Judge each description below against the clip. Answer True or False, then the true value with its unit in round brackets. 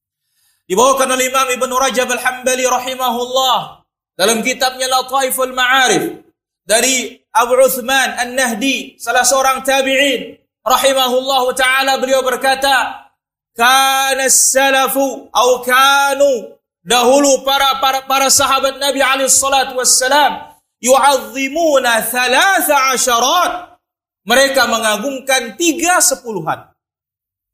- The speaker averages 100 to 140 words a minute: False (90 wpm)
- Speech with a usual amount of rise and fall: False (1.2 semitones)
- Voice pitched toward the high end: True (265 Hz)